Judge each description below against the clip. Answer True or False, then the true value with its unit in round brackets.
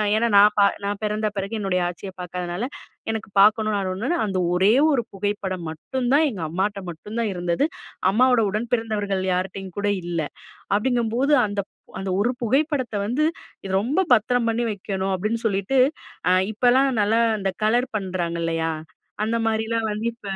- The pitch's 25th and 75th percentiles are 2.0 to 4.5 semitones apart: True (3.3 semitones)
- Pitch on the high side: True (210 Hz)